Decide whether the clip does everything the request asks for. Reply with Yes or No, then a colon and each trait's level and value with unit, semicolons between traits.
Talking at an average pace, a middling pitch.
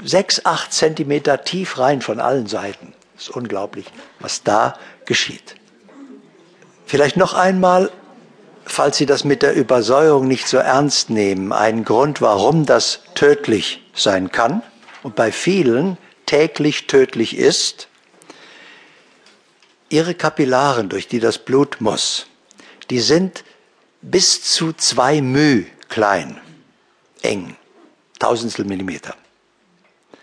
No: slow, 115 wpm; medium, 145 Hz